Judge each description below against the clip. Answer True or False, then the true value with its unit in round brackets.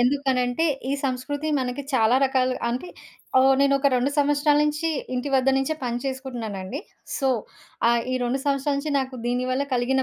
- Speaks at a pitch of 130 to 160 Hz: False (265 Hz)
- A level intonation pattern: True (2.2 semitones)